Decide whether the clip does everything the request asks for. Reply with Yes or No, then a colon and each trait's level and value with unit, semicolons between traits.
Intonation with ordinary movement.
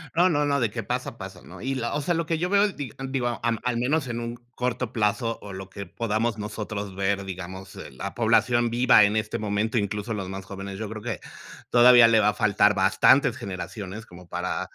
Yes: average, 3.6 semitones